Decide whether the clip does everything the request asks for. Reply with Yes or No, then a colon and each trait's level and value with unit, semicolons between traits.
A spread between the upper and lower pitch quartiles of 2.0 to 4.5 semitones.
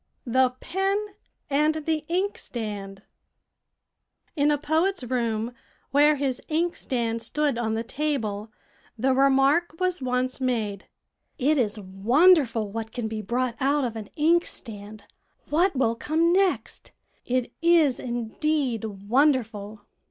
No: wide, 5.4 semitones